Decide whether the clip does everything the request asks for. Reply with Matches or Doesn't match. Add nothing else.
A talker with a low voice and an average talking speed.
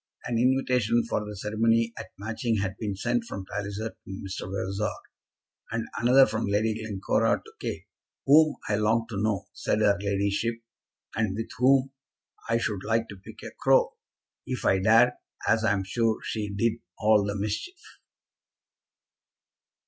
Matches